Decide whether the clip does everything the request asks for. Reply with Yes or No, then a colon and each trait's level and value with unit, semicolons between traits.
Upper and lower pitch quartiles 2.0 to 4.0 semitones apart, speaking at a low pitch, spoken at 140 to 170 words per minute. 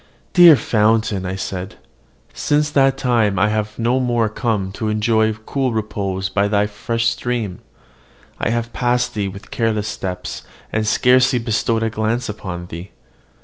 Yes: average, 2.8 semitones; low, 110 Hz; average, 150 wpm